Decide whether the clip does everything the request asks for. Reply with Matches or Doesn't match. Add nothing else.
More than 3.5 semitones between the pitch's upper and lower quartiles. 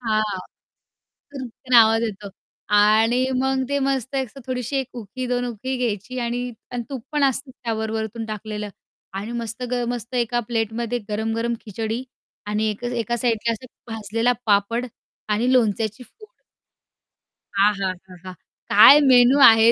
Doesn't match